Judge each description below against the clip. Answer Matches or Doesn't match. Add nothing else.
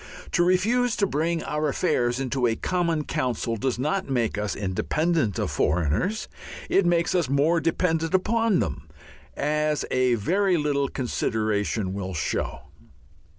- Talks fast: Doesn't match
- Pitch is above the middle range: Doesn't match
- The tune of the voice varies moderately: Doesn't match